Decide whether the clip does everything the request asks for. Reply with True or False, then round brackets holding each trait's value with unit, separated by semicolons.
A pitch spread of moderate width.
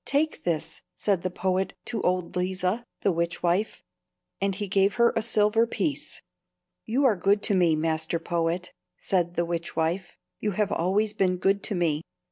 True (3.4 semitones)